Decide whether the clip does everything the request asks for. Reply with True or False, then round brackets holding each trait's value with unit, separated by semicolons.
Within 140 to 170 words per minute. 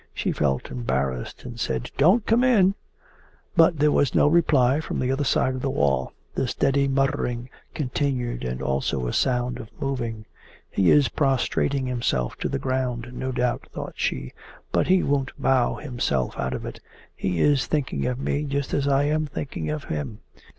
False (180 wpm)